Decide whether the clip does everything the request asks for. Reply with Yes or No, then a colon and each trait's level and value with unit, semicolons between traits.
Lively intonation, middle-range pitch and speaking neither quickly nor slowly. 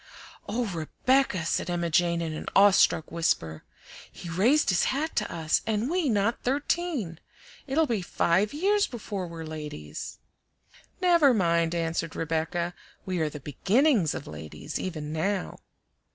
Yes: wide, 7.0 semitones; medium, 180 Hz; average, 145 wpm